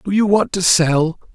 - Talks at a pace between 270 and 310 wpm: No, fast, 225 wpm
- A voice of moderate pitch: Yes, medium, 180 Hz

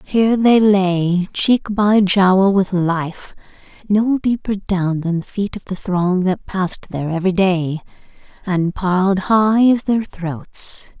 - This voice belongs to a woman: Yes, female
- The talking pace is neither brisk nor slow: Yes, average, 155 wpm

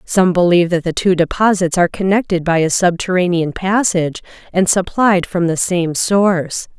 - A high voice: No, medium, 180 Hz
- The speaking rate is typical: Yes, average, 160 wpm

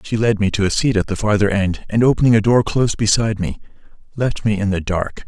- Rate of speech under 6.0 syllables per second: No, 6.1 syllables/s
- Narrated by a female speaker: No, male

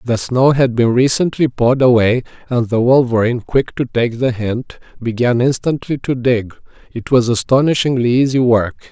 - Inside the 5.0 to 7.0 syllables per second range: Yes, 5.1 syllables/s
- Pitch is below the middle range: Yes, low, 125 Hz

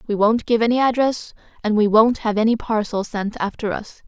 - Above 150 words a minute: Yes, fast, 205 wpm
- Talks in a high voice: Yes, high, 220 Hz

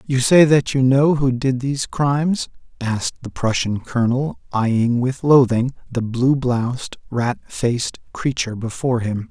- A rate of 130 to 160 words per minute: Yes, average, 155 wpm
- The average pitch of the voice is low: Yes, low, 125 Hz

